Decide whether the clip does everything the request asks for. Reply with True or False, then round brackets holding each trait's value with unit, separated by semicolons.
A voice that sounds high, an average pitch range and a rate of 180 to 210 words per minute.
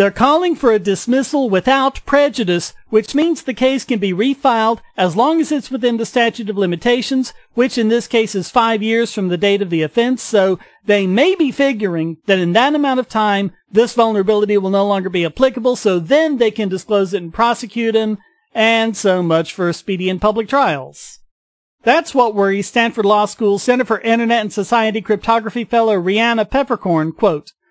True (225 Hz; 3.8 semitones; 190 wpm)